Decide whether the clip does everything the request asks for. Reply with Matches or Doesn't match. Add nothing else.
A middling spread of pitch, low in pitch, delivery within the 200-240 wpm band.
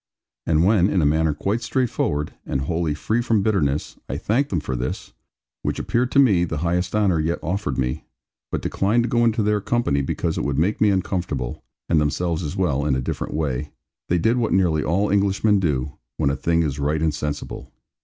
Doesn't match